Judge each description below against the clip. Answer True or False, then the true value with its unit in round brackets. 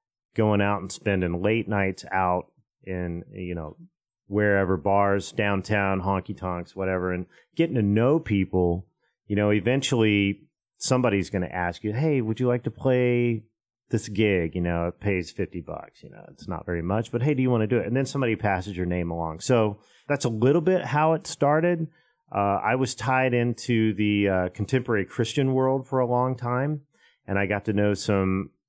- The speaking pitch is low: True (105 Hz)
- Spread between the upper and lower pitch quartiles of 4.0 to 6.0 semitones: True (4.7 semitones)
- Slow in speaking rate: False (190 wpm)